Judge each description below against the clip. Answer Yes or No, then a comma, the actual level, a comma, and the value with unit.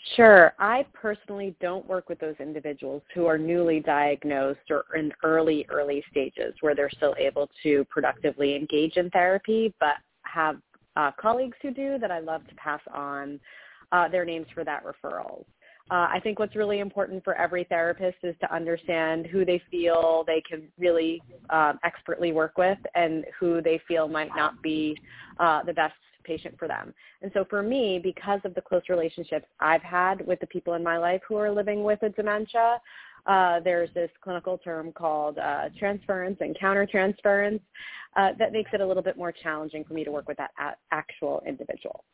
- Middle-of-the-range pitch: Yes, medium, 170 Hz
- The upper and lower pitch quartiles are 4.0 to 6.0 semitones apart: No, average, 3.5 semitones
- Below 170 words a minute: No, average, 185 wpm